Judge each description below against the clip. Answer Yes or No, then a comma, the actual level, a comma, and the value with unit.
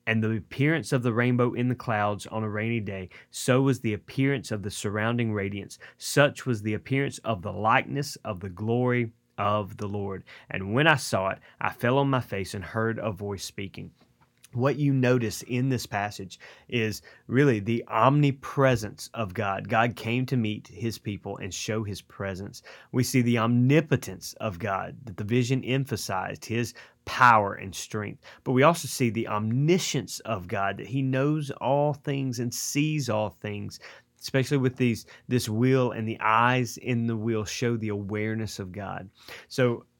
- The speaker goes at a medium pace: Yes, average, 180 wpm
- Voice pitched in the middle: No, low, 115 Hz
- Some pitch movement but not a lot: Yes, average, 3.6 semitones